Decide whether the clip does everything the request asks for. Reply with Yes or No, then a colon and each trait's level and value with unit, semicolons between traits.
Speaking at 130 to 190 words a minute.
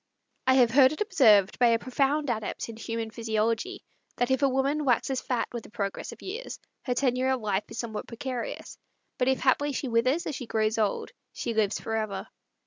No: average, 200 wpm